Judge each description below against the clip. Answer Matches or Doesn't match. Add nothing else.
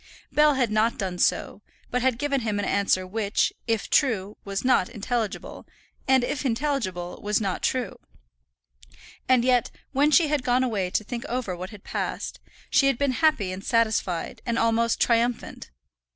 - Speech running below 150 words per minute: Doesn't match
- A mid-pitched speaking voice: Doesn't match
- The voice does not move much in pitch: Doesn't match